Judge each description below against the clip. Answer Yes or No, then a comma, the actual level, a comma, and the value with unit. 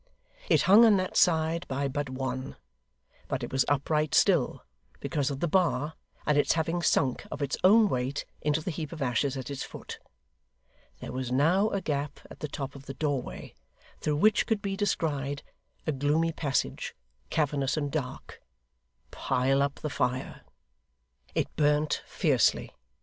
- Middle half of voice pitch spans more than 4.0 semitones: No, average, 3.1 semitones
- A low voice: No, medium, 145 Hz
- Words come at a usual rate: Yes, average, 160 wpm